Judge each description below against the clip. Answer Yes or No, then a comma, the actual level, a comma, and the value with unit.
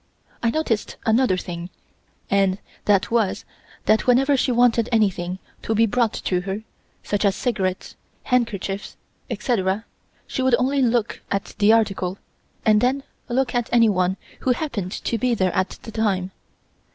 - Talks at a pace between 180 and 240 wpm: No, average, 150 wpm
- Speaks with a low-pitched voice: No, high, 220 Hz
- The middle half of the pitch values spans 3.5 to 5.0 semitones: Yes, average, 4.0 semitones